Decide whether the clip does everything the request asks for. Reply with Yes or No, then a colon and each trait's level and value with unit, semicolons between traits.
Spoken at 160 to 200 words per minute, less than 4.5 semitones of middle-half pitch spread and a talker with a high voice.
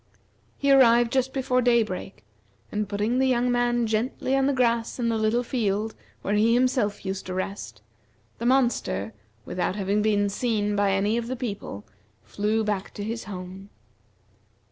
Yes: average, 165 wpm; average, 3.2 semitones; high, 220 Hz